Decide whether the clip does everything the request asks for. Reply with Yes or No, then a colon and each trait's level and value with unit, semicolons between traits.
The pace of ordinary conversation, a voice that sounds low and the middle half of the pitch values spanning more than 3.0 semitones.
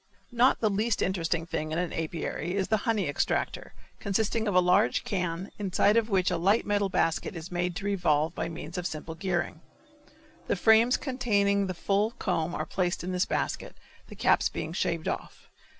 No: average, 190 wpm; medium, 185 Hz; average, 3.4 semitones